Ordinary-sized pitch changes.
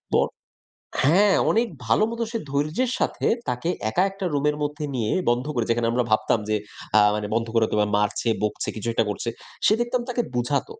No: wide, 9.0 semitones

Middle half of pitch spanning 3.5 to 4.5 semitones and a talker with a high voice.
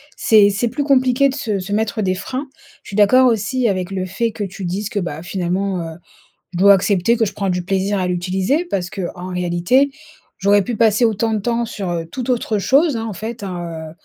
Yes: average, 4.1 semitones; high, 200 Hz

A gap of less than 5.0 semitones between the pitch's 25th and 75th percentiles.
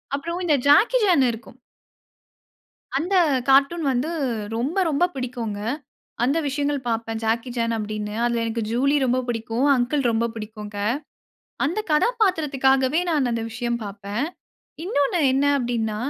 Yes: average, 4.2 semitones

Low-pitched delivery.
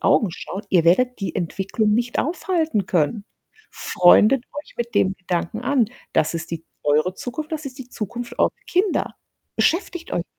No: high, 220 Hz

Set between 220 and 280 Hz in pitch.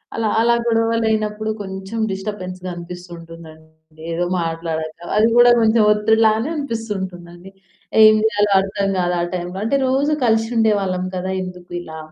No: high, 195 Hz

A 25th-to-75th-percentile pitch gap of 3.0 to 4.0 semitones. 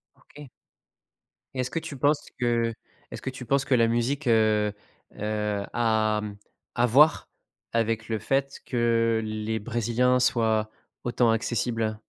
No: narrow, 2.4 semitones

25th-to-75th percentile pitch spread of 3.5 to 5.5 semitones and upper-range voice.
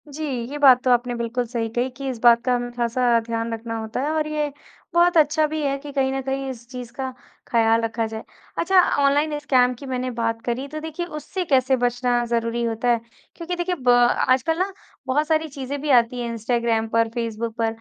Yes: average, 3.8 semitones; very high, 250 Hz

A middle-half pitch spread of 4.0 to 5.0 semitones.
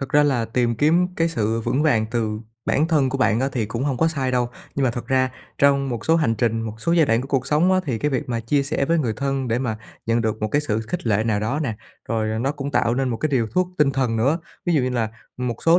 Yes: average, 4.3 semitones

